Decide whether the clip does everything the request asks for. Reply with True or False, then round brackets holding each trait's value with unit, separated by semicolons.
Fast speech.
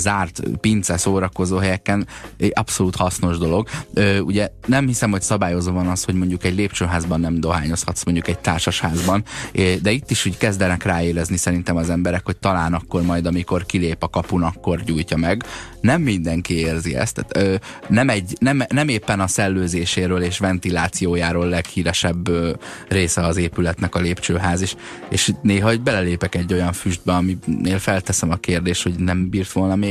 True (170 wpm)